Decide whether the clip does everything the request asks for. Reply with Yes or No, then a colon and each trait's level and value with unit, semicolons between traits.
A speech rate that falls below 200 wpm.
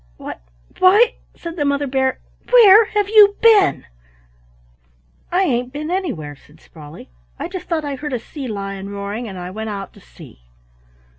Yes: average, 165 wpm